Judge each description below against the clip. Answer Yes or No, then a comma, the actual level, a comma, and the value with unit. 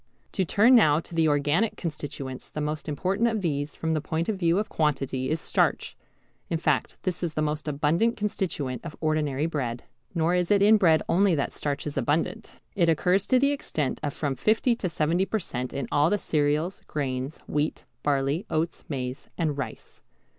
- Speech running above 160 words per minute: Yes, average, 190 wpm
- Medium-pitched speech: Yes, medium, 155 Hz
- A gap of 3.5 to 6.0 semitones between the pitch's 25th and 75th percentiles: Yes, average, 4.1 semitones